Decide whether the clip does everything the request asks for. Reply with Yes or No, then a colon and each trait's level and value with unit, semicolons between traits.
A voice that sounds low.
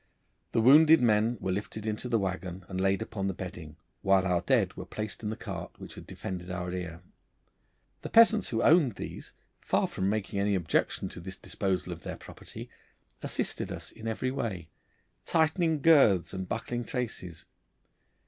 Yes: low, 100 Hz